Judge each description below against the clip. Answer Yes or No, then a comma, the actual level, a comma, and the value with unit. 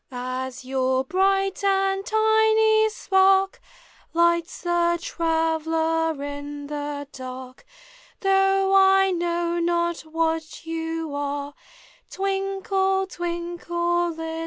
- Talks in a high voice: Yes, very high, 340 Hz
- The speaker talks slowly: Yes, slow, 95 wpm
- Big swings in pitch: No, average, 3.6 semitones